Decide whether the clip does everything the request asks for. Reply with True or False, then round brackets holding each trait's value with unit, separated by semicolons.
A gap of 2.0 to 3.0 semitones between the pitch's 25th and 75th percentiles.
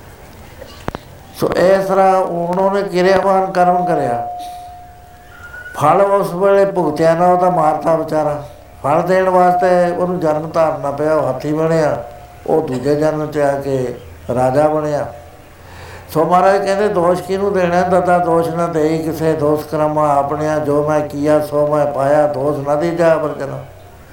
False (3.6 semitones)